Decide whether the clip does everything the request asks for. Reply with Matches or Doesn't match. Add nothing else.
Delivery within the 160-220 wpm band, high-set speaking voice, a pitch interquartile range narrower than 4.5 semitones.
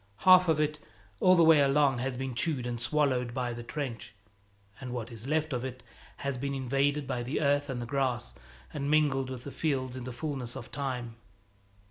Doesn't match